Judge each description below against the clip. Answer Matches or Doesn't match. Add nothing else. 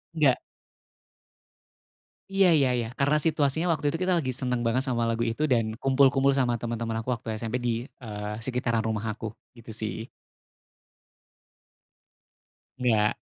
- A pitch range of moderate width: Matches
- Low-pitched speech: Matches